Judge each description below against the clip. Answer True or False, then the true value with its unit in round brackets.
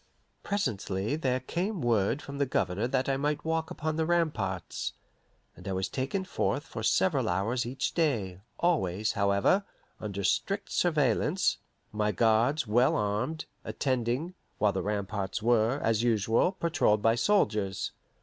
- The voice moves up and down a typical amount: False (6.9 semitones)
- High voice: False (120 Hz)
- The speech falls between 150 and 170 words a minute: False (140 wpm)